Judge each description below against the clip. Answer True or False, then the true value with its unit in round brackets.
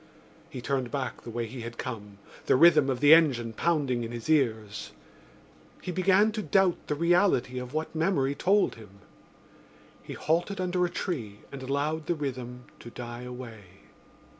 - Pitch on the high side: False (135 Hz)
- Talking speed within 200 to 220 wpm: False (165 wpm)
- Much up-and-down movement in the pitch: True (6.1 semitones)